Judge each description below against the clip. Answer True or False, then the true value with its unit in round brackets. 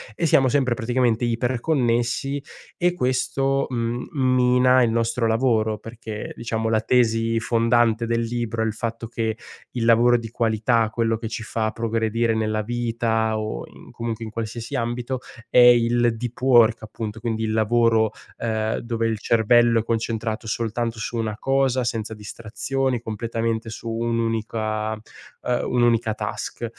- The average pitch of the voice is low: True (115 Hz)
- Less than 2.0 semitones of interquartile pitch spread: True (1.4 semitones)